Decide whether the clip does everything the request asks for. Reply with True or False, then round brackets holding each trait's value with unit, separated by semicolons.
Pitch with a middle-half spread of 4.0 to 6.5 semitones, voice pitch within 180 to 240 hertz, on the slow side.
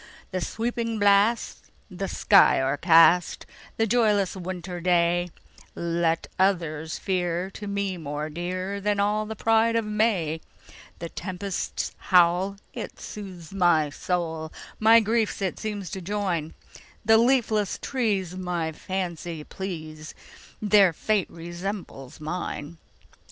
False (3.6 semitones; 185 Hz; 100 wpm)